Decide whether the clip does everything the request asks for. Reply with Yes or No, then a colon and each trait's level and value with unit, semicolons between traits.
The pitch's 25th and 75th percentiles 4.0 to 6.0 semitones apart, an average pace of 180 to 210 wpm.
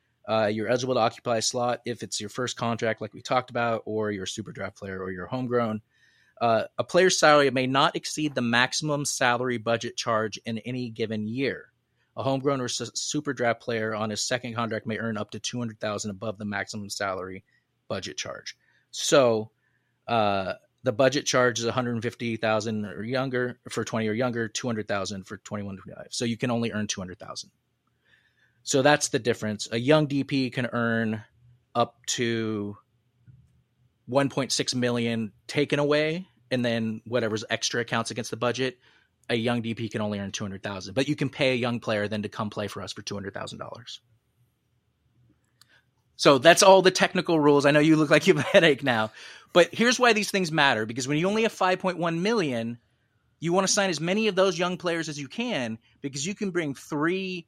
Yes: average, 4.3 semitones; average, 185 wpm